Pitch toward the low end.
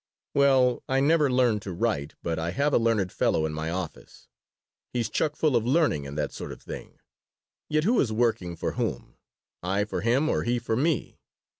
Yes: low, 115 Hz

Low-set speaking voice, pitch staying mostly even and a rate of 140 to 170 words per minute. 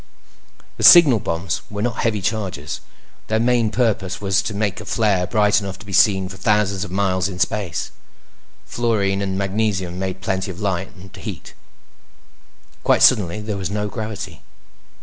Yes: low, 100 Hz; narrow, 2.2 semitones; average, 160 wpm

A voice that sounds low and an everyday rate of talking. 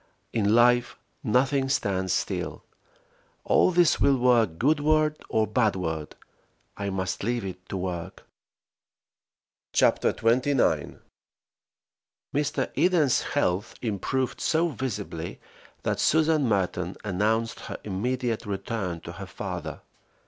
No: low, 115 Hz; slow, 105 wpm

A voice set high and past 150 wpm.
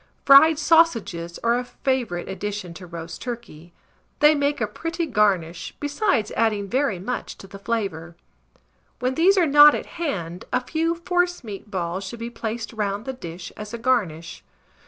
Yes: high, 230 Hz; average, 160 wpm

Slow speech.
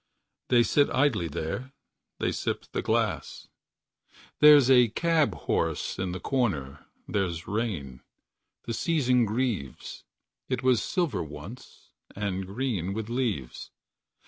Yes: slow, 120 wpm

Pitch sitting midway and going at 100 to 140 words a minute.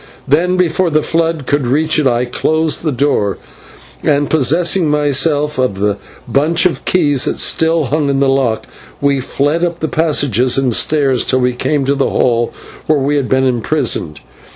No: medium, 145 Hz; average, 175 wpm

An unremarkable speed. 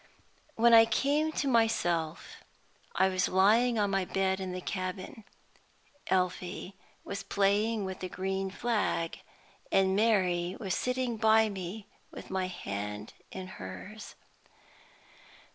No: slow, 125 wpm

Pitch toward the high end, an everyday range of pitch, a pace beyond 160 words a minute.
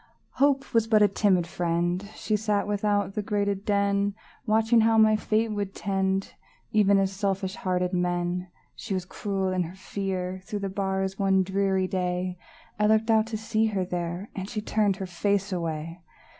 No: high, 195 Hz; narrow, 2.2 semitones; average, 175 wpm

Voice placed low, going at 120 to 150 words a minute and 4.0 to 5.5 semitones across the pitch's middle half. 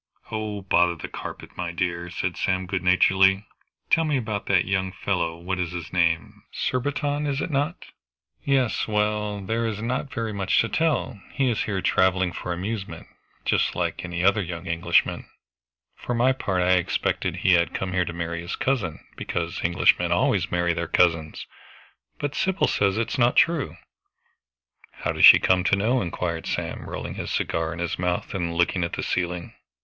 No: very low, 95 Hz; average, 180 wpm; average, 4.3 semitones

